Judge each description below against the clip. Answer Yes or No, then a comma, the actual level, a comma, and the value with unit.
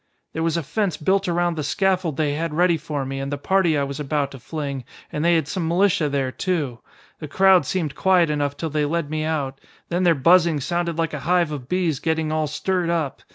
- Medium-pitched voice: Yes, medium, 160 Hz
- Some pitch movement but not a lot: Yes, average, 3.1 semitones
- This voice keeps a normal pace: No, fast, 230 wpm